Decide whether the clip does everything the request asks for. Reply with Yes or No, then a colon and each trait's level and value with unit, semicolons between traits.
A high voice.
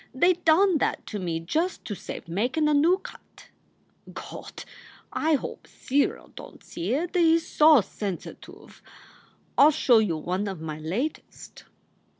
Yes: very high, 275 Hz